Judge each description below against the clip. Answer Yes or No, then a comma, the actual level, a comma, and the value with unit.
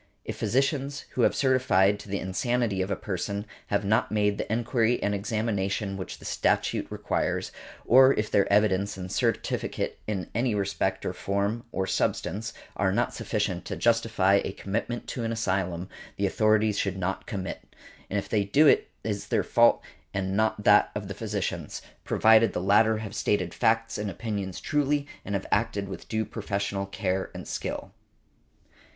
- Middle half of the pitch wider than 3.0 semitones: No, narrow, 2.6 semitones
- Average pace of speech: Yes, average, 170 wpm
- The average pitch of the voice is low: Yes, low, 105 Hz